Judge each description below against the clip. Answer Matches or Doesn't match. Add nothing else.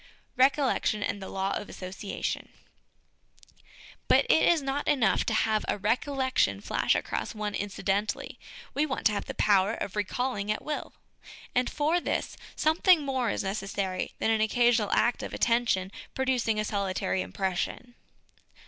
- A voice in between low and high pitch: Doesn't match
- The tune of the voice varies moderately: Matches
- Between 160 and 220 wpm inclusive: Doesn't match